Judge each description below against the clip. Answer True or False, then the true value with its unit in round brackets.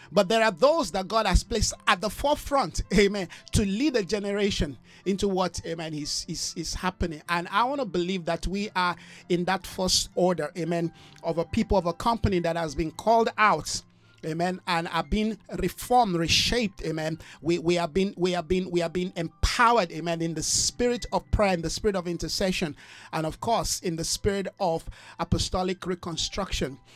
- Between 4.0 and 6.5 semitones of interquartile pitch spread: False (3.6 semitones)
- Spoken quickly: False (190 wpm)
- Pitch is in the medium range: True (180 Hz)